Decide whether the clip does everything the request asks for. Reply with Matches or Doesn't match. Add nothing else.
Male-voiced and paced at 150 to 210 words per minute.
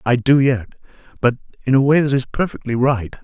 Matches